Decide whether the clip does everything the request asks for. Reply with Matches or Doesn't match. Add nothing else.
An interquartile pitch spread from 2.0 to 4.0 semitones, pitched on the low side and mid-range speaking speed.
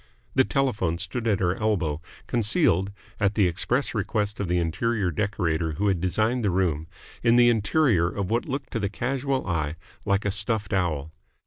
Doesn't match